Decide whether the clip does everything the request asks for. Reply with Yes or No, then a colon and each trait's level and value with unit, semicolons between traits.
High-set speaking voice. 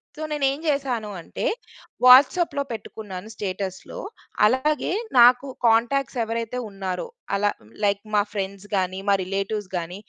Yes: high, 220 Hz